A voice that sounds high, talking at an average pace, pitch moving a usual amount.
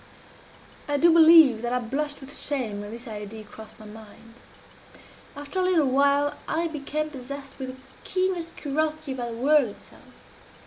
Yes: very high, 280 Hz; average, 165 wpm; average, 4.5 semitones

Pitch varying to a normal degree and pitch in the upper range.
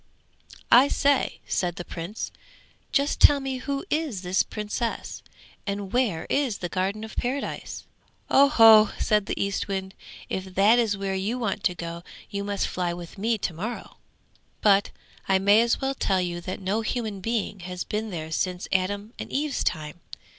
Yes: average, 3.9 semitones; high, 200 Hz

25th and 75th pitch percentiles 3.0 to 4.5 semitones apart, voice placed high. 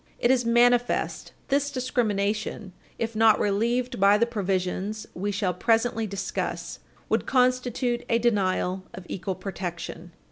Yes: average, 3.8 semitones; high, 215 Hz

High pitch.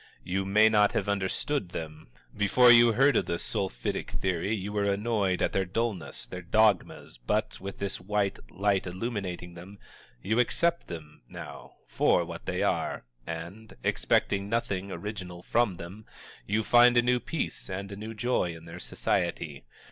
No: low, 100 Hz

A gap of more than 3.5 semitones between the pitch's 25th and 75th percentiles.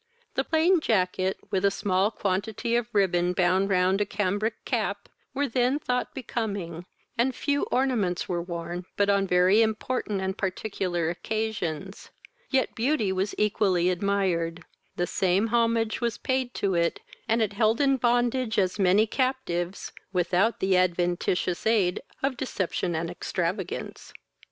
Yes: average, 4.2 semitones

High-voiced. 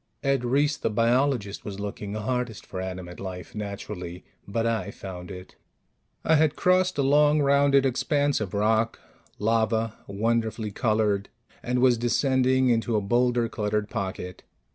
No: low, 115 Hz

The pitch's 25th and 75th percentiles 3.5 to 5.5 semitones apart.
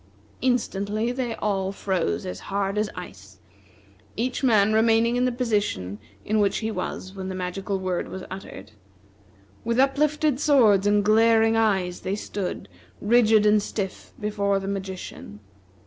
No: average, 3.0 semitones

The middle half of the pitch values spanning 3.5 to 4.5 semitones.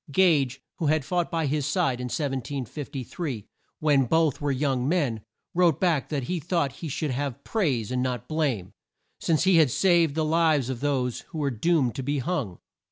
Yes: average, 4.0 semitones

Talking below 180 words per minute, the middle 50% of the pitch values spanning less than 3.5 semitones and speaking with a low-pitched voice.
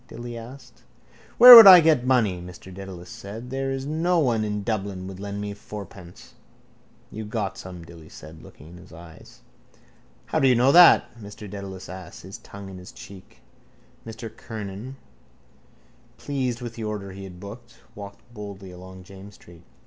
No: average, 170 wpm; average, 4.4 semitones; low, 100 Hz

